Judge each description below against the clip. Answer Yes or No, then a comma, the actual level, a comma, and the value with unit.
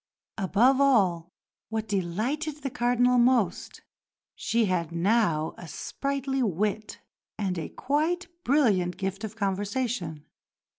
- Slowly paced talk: Yes, slow, 115 wpm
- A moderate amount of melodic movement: No, wide, 5.9 semitones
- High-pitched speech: Yes, high, 220 Hz